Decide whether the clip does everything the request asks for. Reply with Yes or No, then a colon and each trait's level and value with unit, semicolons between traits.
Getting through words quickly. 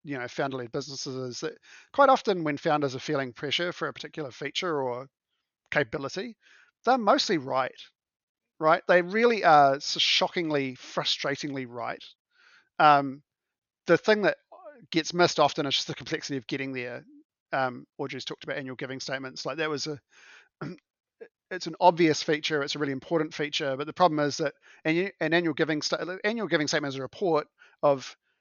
No: average, 165 wpm